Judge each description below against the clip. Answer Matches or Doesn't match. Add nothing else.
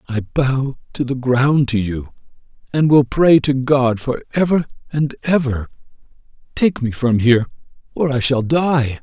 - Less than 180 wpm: Matches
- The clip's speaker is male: Matches